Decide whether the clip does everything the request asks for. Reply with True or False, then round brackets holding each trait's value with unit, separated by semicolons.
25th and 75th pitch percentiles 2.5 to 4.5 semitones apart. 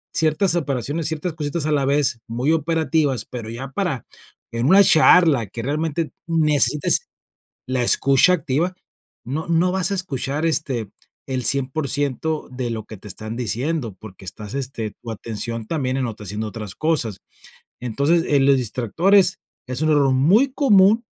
False (5.3 semitones)